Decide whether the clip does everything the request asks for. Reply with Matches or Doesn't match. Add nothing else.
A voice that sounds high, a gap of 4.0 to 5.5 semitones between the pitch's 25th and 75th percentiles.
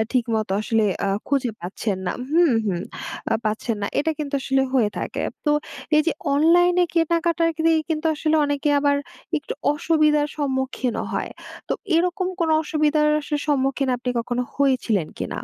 Matches